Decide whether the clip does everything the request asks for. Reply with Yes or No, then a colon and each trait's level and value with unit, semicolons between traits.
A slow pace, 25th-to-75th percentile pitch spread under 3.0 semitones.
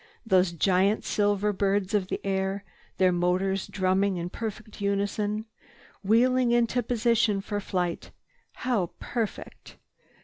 Yes: slow, 110 wpm; narrow, 2.5 semitones